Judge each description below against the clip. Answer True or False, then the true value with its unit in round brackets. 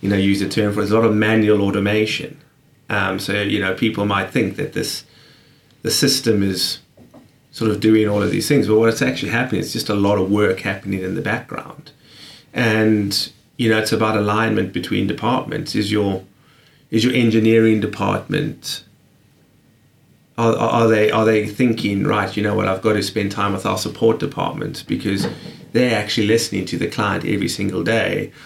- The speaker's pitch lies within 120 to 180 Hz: False (110 Hz)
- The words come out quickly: False (185 wpm)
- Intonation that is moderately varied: False (2.1 semitones)